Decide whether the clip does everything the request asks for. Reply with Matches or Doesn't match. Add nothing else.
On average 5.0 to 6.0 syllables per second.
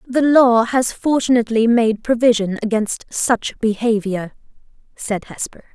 Doesn't match